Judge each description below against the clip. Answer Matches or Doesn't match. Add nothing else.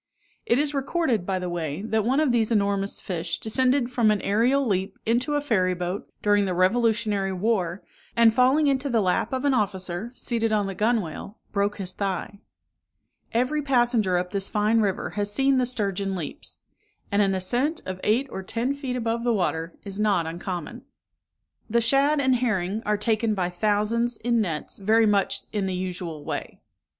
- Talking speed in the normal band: Matches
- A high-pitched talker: Matches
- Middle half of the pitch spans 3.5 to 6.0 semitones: Matches